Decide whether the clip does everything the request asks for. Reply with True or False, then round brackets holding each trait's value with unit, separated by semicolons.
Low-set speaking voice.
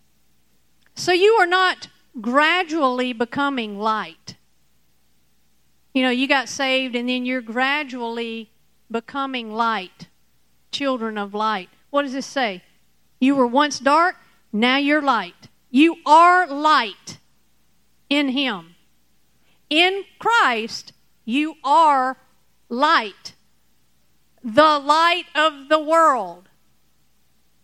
False (270 Hz)